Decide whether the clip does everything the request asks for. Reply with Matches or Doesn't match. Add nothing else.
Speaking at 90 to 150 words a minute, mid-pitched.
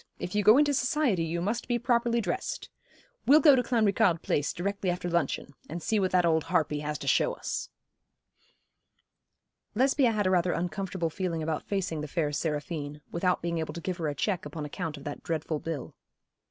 Doesn't match